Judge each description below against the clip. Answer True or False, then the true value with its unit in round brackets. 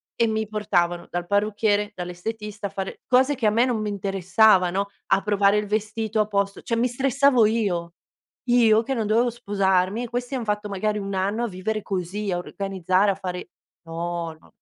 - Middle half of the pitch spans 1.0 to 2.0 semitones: False (2.6 semitones)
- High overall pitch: True (210 Hz)